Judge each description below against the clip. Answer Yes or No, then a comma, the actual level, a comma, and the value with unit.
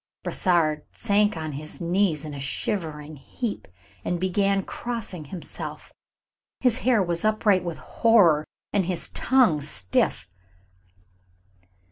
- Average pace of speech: No, slow, 115 wpm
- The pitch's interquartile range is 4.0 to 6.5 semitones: Yes, average, 5.2 semitones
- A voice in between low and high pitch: Yes, medium, 180 Hz